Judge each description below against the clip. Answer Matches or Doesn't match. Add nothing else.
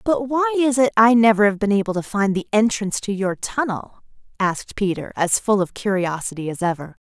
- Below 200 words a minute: Doesn't match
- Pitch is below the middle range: Doesn't match